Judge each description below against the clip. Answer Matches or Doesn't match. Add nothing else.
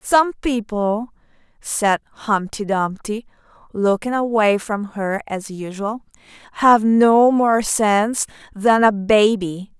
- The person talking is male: Doesn't match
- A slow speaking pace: Matches